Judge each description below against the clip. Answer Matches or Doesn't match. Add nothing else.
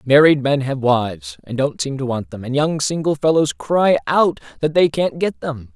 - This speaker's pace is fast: Matches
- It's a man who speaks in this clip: Matches